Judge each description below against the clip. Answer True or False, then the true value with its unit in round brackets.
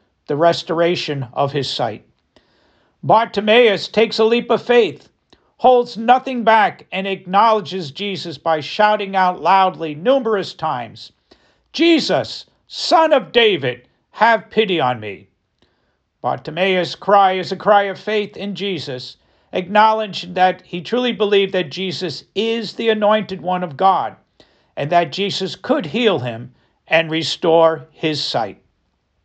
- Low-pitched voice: False (190 Hz)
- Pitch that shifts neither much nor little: True (5.0 semitones)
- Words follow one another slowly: True (130 wpm)